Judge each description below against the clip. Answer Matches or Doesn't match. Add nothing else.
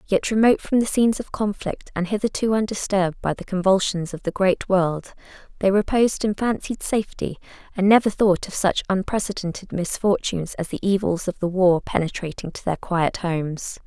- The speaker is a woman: Matches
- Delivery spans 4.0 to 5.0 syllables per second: Doesn't match